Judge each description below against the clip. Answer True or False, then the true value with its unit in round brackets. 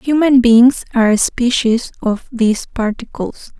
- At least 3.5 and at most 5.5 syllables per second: True (4.4 syllables/s)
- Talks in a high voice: True (240 Hz)